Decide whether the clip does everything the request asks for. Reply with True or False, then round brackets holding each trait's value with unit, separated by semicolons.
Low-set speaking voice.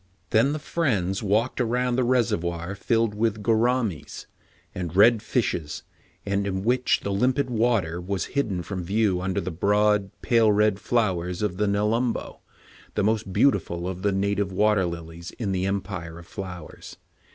True (100 Hz)